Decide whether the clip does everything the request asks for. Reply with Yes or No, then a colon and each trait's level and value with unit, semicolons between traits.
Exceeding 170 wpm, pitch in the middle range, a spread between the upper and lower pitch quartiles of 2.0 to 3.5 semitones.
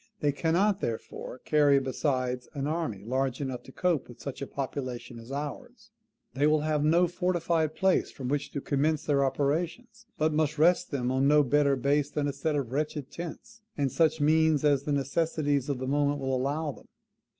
Yes: average, 190 wpm; medium, 145 Hz; average, 2.7 semitones